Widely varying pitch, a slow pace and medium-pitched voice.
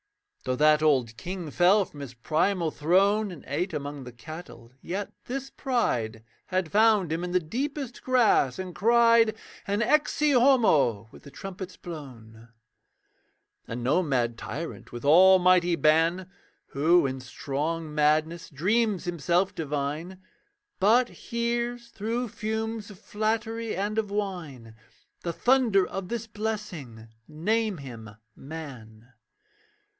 Yes: wide, 7.1 semitones; slow, 130 wpm; medium, 175 Hz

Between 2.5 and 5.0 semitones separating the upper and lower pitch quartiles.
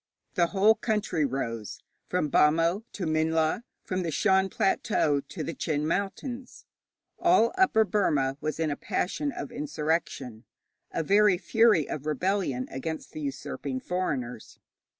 No: wide, 5.4 semitones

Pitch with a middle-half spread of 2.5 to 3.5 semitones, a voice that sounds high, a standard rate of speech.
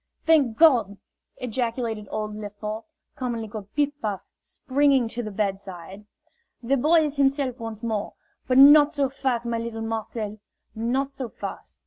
No: average, 4.1 semitones; high, 235 Hz; average, 145 wpm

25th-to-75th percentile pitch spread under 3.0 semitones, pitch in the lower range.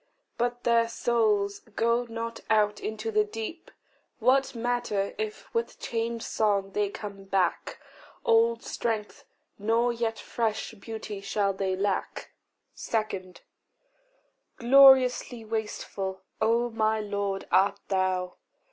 No: narrow, 2.6 semitones; high, 220 Hz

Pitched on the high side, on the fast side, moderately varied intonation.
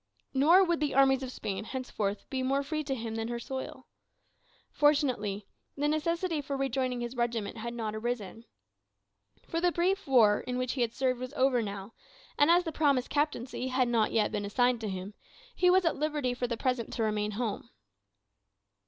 No: very high, 255 Hz; average, 190 wpm; average, 4.3 semitones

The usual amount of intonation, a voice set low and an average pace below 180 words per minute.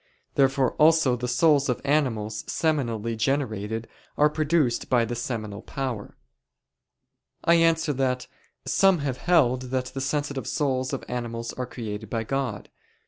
Yes: average, 3.8 semitones; low, 130 Hz; average, 140 wpm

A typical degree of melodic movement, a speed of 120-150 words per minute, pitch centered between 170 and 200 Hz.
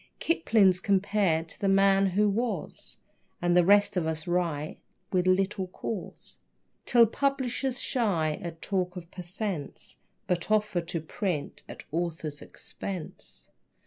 Yes: average, 3.3 semitones; slow, 135 wpm; medium, 185 Hz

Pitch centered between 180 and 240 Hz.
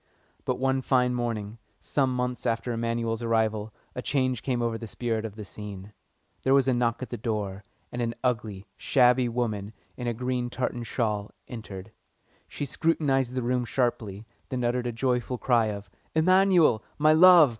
No: low, 120 Hz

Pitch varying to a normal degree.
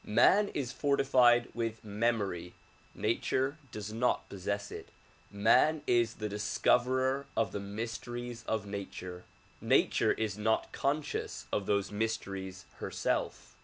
Yes: average, 3.4 semitones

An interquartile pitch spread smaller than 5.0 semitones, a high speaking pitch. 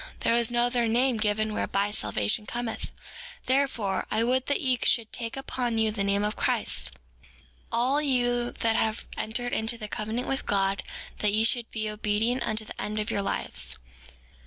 Yes: narrow, 2.4 semitones; high, 225 Hz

